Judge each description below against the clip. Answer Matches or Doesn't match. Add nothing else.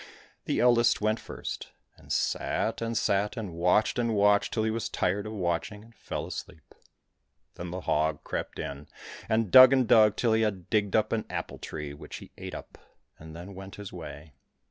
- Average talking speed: Matches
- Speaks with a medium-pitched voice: Doesn't match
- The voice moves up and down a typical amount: Matches